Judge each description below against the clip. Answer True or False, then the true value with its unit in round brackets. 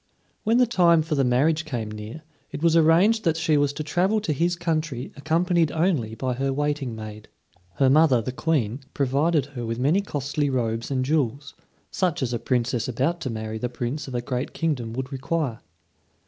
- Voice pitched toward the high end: False (140 Hz)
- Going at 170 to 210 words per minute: True (190 wpm)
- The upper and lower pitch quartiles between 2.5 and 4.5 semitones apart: False (4.9 semitones)